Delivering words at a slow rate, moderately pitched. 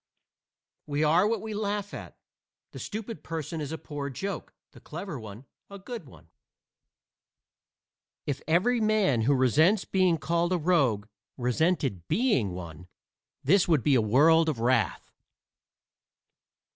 Yes: slow, 130 wpm; medium, 160 Hz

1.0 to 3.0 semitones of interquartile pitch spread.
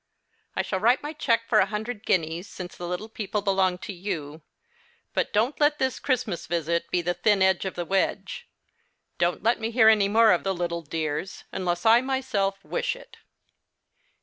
No: average, 4.4 semitones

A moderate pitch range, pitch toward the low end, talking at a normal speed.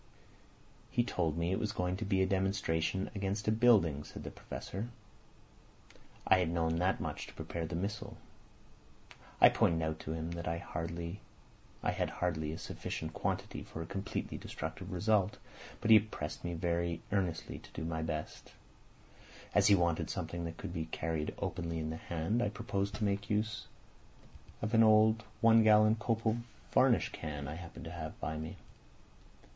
Yes: average, 4.2 semitones; very low, 90 Hz; average, 170 wpm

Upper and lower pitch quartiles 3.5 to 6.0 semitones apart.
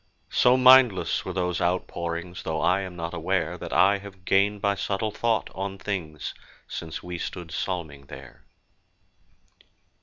No: average, 3.0 semitones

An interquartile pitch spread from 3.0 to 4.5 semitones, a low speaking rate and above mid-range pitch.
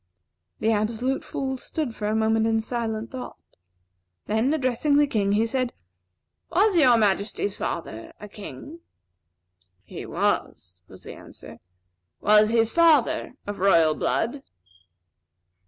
Yes: average, 4.1 semitones; slow, 125 wpm; high, 225 Hz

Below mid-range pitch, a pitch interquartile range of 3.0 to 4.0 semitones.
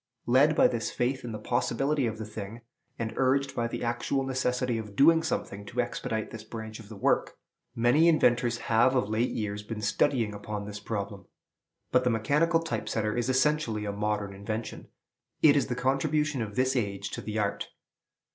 Yes: low, 115 Hz; average, 3.7 semitones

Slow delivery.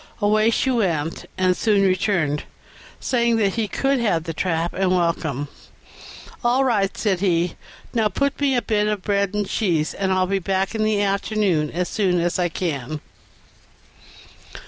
No: average, 170 wpm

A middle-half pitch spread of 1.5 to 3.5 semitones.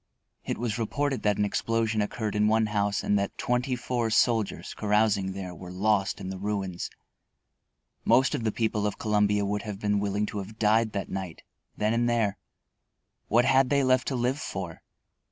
Yes: narrow, 2.4 semitones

